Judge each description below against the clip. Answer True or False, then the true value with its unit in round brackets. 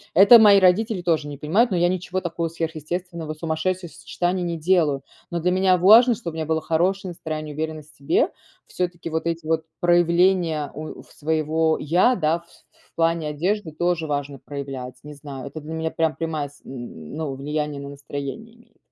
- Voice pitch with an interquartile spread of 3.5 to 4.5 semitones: False (3.0 semitones)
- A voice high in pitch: False (160 Hz)